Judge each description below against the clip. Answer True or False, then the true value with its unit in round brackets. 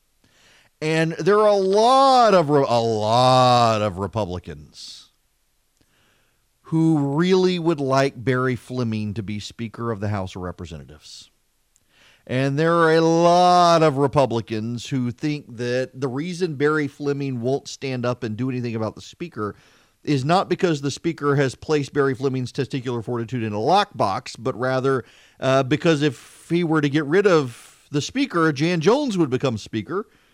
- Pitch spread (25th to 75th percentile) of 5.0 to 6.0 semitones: True (5.5 semitones)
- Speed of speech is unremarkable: True (155 wpm)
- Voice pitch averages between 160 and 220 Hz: False (135 Hz)